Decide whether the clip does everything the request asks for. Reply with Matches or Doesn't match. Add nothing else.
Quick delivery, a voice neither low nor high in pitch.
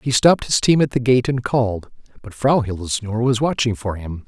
Doesn't match